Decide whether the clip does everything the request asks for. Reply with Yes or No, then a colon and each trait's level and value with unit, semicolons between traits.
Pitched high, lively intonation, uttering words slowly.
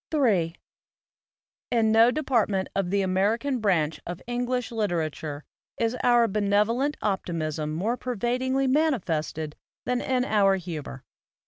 Yes: high, 210 Hz; wide, 5.9 semitones; slow, 115 wpm